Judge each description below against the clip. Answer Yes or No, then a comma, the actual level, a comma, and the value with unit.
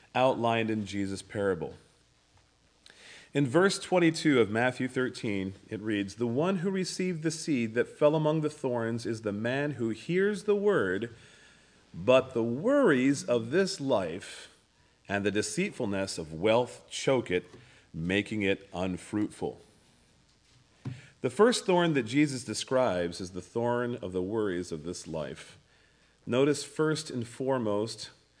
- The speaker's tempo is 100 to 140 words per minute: Yes, slow, 135 wpm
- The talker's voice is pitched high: No, low, 120 Hz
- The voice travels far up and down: Yes, wide, 6.5 semitones